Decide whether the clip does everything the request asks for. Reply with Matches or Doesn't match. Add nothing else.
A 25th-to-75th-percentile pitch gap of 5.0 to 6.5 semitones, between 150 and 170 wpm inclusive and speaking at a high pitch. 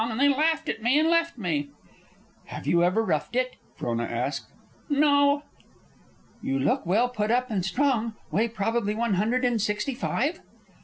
Matches